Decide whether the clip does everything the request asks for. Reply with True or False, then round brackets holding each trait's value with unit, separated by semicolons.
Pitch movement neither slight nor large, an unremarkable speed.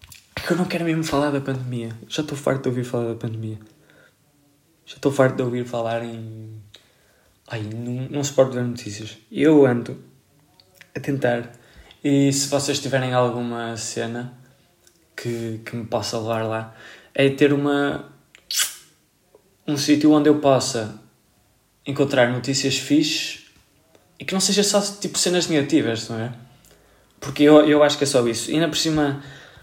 True (4.0 semitones; 160 wpm)